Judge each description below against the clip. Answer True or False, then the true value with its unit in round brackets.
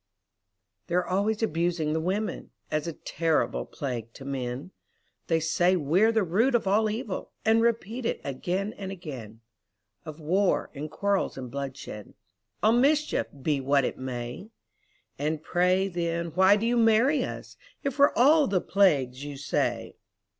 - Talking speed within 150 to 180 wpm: True (155 wpm)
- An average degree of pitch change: False (6.8 semitones)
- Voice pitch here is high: False (175 Hz)